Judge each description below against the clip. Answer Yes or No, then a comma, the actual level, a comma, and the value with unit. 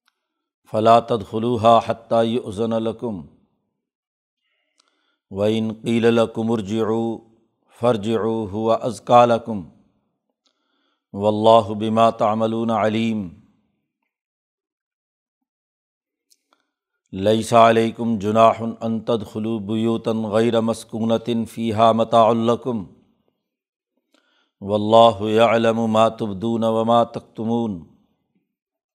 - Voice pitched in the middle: No, low, 115 Hz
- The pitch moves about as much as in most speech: No, narrow, 0.8 semitones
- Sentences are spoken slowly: Yes, slow, 50 wpm